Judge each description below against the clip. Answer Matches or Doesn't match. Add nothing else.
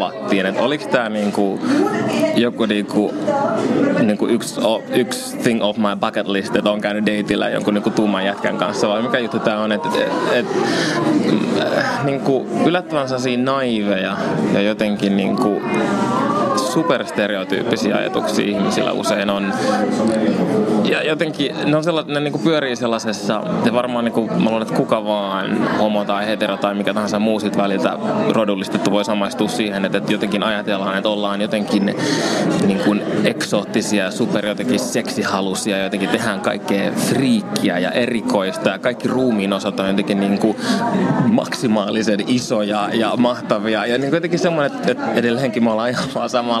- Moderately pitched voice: Doesn't match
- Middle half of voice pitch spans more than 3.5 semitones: Doesn't match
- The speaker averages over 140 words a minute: Matches